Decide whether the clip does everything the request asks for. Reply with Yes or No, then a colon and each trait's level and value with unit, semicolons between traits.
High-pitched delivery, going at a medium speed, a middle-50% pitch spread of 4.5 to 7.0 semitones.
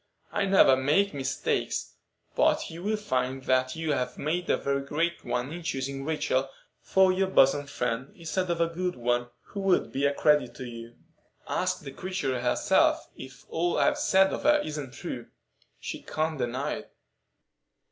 No: medium, 145 Hz; average, 165 wpm; average, 5.2 semitones